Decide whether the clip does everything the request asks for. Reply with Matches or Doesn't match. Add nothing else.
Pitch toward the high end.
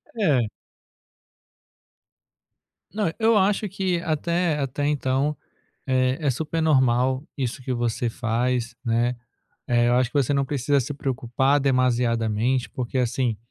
Doesn't match